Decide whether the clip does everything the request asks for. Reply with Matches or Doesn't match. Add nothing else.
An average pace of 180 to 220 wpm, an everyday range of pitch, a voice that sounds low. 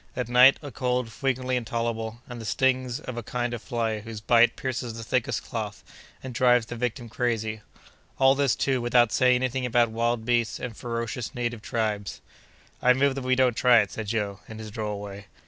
Doesn't match